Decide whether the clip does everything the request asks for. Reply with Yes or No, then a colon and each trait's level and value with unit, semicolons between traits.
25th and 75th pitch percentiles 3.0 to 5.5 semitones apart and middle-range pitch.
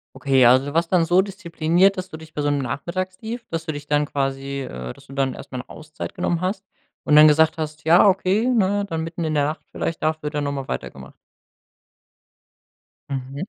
Yes: average, 4.2 semitones; medium, 155 Hz